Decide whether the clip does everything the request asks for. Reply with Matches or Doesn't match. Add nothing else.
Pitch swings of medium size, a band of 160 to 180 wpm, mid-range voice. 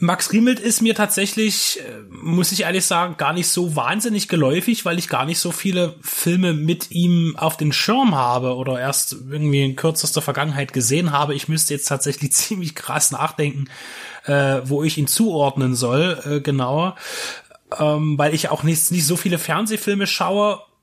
Matches